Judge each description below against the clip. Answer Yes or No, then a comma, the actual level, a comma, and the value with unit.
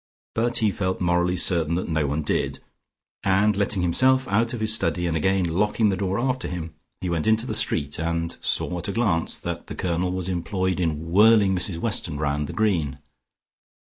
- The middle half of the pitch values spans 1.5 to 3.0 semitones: No, average, 4.2 semitones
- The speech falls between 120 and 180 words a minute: No, average, 195 wpm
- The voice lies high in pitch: No, very low, 95 Hz